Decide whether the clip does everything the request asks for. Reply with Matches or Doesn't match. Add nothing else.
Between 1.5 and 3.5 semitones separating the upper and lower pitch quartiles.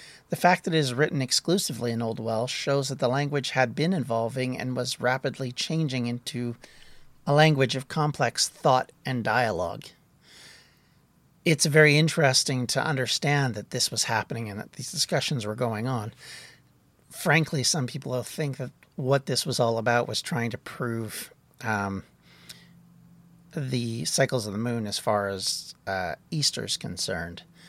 Doesn't match